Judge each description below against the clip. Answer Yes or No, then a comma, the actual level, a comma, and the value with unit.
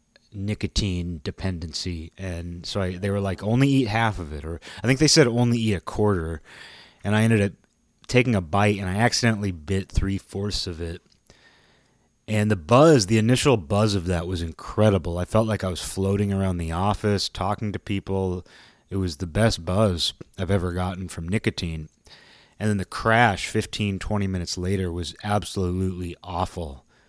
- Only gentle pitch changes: No, average, 3.1 semitones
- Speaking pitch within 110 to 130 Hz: No, very low, 95 Hz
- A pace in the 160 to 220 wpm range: Yes, average, 175 wpm